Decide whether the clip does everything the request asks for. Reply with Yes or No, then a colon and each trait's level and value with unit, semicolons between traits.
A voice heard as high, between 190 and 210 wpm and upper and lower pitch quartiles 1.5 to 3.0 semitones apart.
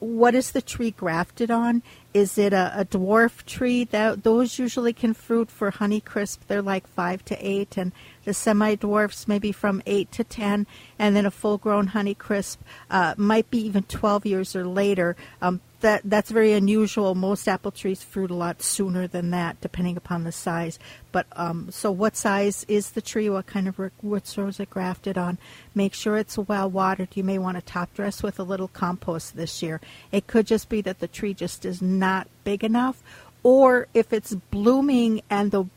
Yes: high, 200 Hz; average, 200 wpm; narrow, 2.5 semitones